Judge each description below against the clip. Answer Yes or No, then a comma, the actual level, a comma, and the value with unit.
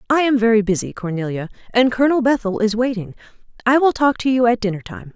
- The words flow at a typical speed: No, fast, 210 wpm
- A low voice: No, high, 230 Hz